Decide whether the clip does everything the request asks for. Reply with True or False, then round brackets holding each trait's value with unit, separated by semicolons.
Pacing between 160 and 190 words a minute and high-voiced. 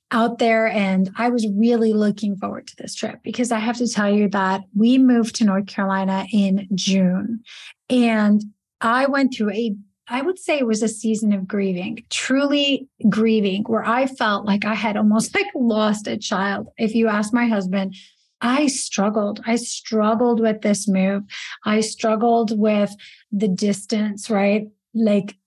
True (165 wpm; 215 Hz)